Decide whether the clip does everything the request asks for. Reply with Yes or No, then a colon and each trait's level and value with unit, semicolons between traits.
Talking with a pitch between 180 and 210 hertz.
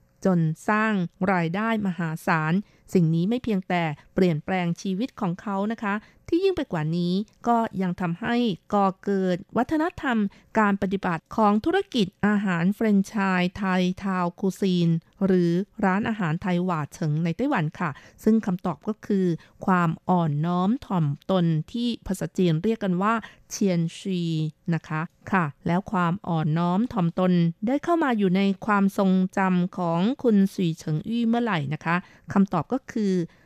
Yes: high, 190 Hz